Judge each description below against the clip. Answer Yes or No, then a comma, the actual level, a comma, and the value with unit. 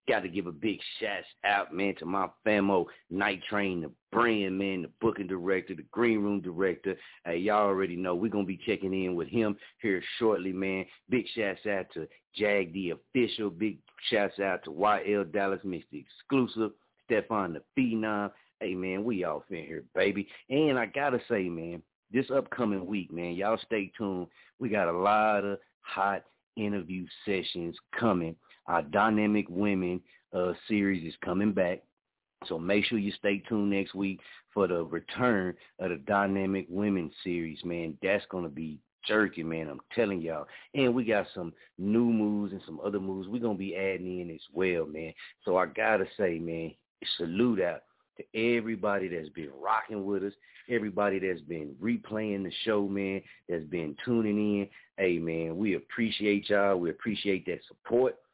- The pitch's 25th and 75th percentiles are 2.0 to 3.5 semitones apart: Yes, average, 2.8 semitones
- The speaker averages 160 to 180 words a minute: Yes, average, 175 wpm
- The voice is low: Yes, low, 100 Hz